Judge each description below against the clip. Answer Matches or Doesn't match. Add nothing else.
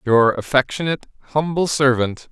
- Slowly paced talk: Matches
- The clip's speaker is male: Matches